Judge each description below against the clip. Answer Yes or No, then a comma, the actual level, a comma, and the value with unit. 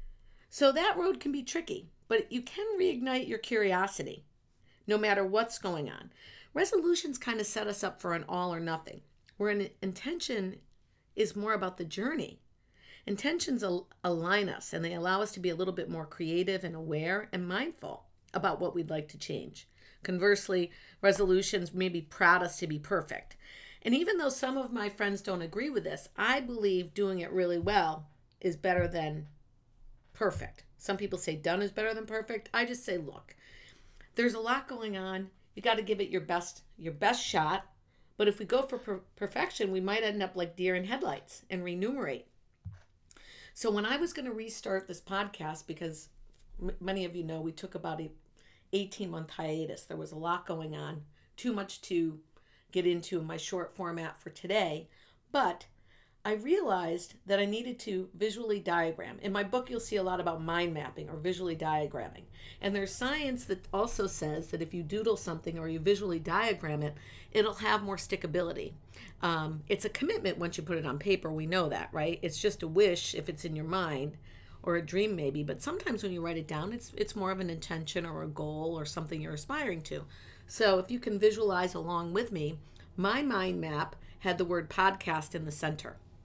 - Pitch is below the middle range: No, medium, 185 Hz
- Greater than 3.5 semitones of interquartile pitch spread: Yes, average, 4.5 semitones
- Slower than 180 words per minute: No, average, 195 wpm